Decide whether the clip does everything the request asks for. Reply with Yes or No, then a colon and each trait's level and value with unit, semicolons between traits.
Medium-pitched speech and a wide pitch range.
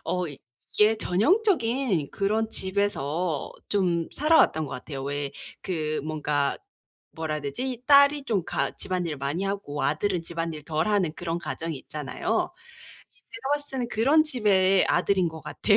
Yes: medium, 180 Hz; wide, 6.5 semitones